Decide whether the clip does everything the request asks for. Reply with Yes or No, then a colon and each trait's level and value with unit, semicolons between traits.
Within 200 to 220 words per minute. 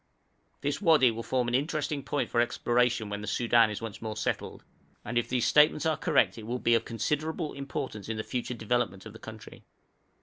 Yes: fast, 205 wpm